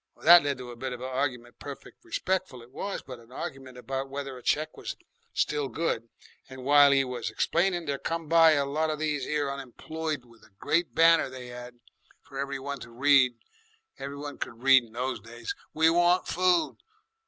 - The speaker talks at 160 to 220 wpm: Yes, average, 200 wpm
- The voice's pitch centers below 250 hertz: Yes, medium, 140 Hz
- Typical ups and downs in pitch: Yes, average, 3.8 semitones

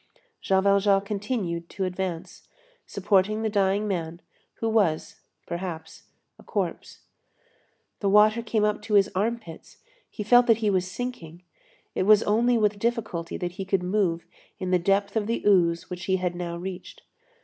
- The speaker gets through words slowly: No, average, 160 wpm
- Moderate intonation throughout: Yes, average, 3.0 semitones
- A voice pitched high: Yes, high, 195 Hz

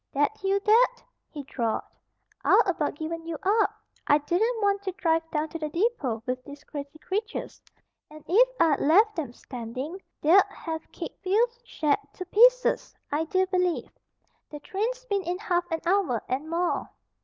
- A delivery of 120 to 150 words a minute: No, average, 165 wpm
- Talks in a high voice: Yes, very high, 345 Hz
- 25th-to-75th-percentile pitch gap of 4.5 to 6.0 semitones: Yes, average, 5.2 semitones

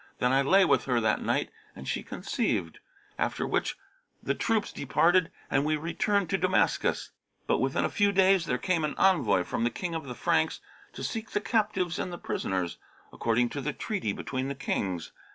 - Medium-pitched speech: Yes, medium, 155 Hz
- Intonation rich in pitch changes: Yes, wide, 7.3 semitones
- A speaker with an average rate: Yes, average, 190 wpm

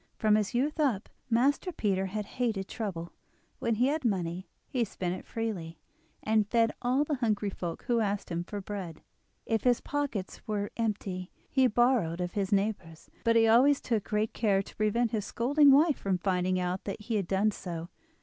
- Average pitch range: Yes, average, 4.1 semitones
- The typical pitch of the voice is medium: No, high, 210 Hz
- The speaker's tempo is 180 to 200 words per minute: Yes, average, 190 wpm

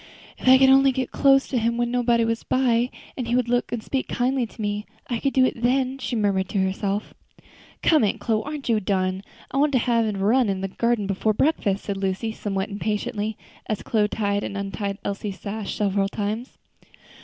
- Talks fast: Yes, fast, 210 wpm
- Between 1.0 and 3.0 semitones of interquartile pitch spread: No, average, 3.6 semitones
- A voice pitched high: Yes, high, 220 Hz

